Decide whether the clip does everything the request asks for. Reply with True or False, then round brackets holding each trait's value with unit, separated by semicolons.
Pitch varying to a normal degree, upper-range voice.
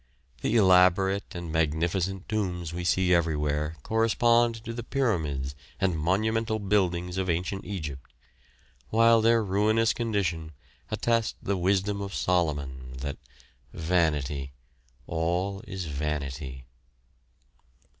False (4.7 semitones; 90 Hz)